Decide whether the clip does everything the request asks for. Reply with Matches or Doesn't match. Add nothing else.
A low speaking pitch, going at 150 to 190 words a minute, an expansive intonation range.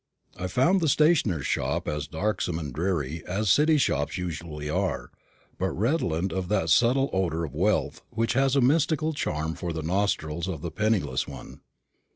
Matches